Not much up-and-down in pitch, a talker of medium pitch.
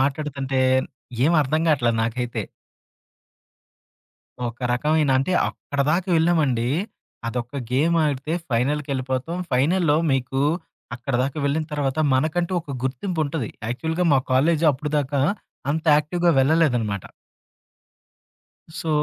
No: average, 3.5 semitones; medium, 145 Hz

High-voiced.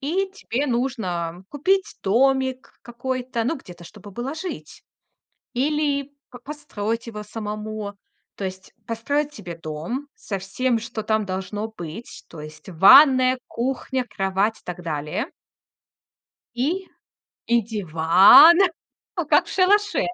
Yes: high, 230 Hz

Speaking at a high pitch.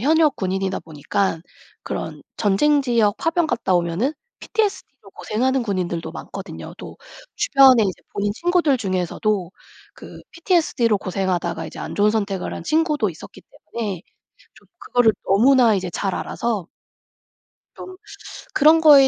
Yes: high, 215 Hz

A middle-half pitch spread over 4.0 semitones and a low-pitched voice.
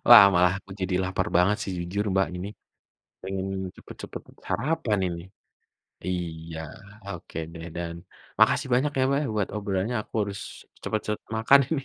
No: average, 3.1 semitones; very low, 95 Hz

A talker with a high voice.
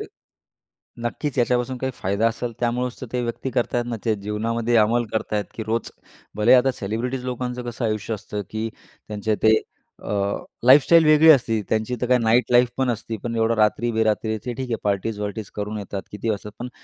No: low, 115 Hz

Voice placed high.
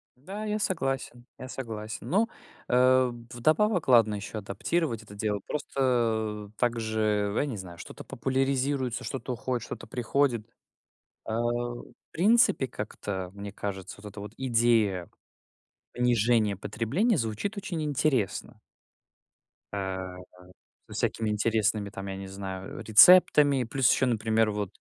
No: low, 115 Hz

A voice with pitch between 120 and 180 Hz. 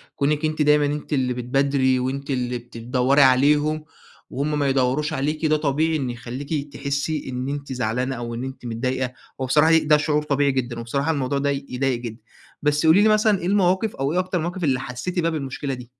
Yes: medium, 140 Hz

